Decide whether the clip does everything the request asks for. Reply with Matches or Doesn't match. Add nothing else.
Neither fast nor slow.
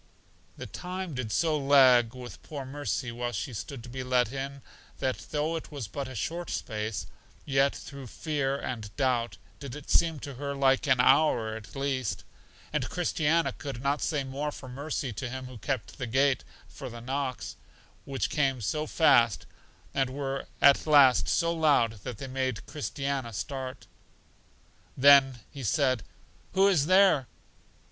Matches